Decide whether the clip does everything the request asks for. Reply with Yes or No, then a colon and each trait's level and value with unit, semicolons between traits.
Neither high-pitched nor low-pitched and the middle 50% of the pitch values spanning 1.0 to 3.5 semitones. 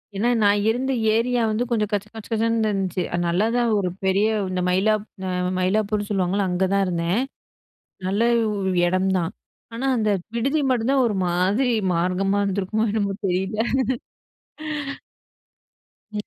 No: high, 205 Hz; average, 3.2 semitones